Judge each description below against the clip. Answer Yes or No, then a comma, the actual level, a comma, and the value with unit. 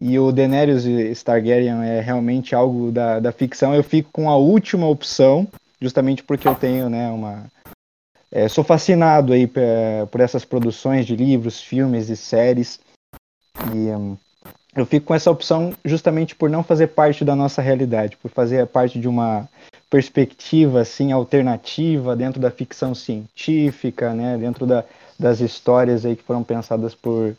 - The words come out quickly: No, average, 155 wpm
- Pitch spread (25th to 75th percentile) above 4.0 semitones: No, average, 3.2 semitones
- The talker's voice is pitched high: No, low, 125 Hz